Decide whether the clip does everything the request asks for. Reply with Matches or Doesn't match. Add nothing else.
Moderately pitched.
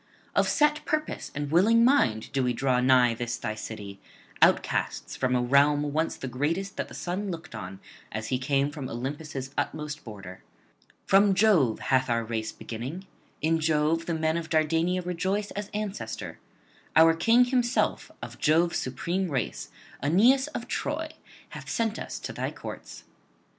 Matches